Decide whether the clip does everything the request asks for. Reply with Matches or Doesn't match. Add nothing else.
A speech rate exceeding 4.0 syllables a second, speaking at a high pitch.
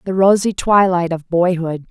Doesn't match